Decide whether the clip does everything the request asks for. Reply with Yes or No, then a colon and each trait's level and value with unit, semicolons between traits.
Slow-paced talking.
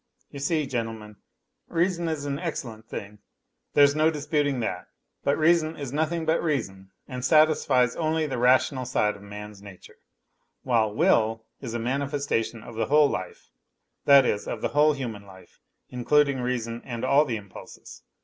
No: average, 160 wpm